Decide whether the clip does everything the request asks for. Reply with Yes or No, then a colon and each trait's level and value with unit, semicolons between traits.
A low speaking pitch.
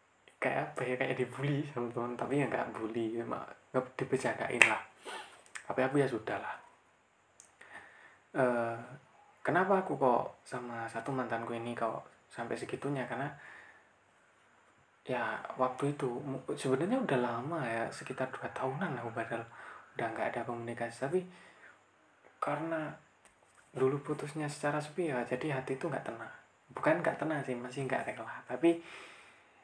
Yes: low, 130 Hz